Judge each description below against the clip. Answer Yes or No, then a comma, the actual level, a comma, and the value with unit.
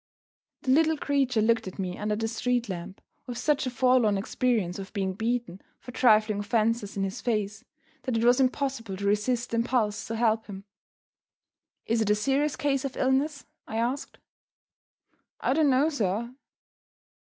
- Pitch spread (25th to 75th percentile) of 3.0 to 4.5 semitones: Yes, average, 3.7 semitones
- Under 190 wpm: Yes, average, 165 wpm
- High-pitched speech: Yes, high, 230 Hz